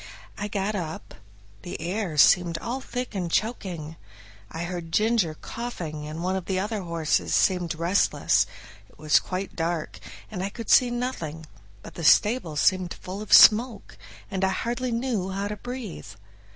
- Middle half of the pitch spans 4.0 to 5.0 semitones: Yes, average, 4.6 semitones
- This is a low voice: No, high, 190 Hz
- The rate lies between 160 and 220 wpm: Yes, average, 165 wpm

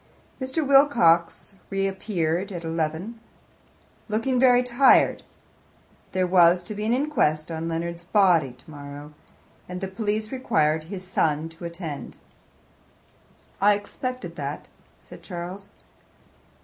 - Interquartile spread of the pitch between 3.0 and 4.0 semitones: No, average, 4.8 semitones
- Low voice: No, medium, 185 Hz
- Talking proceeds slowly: Yes, slow, 110 wpm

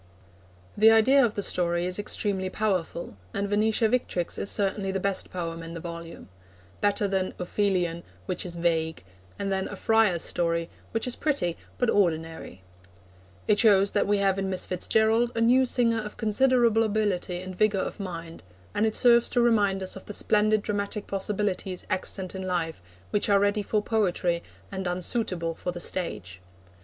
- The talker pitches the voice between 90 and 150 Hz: No, high, 195 Hz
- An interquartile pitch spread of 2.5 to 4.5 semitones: Yes, average, 3.4 semitones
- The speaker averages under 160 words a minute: No, average, 175 wpm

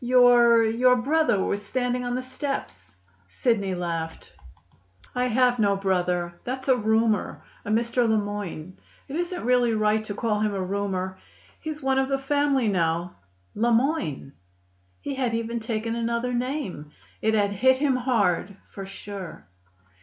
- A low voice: No, high, 230 Hz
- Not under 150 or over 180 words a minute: Yes, average, 155 wpm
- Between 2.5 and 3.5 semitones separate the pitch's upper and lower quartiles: No, average, 4.2 semitones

